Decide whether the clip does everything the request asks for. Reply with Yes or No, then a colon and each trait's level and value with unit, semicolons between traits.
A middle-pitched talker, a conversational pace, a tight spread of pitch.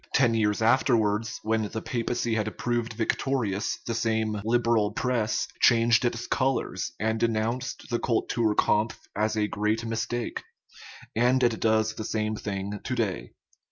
No: low, 110 Hz; average, 155 wpm; narrow, 1.7 semitones